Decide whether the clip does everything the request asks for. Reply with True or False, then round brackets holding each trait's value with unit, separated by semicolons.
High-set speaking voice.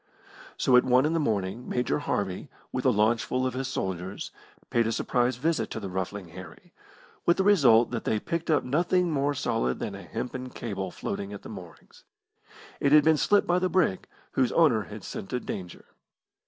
False (125 Hz)